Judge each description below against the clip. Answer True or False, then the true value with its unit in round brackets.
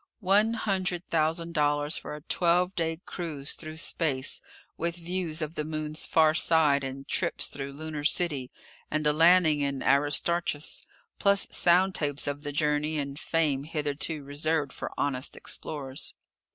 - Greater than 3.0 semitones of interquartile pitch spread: False (2.7 semitones)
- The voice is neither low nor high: True (155 Hz)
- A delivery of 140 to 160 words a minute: True (150 wpm)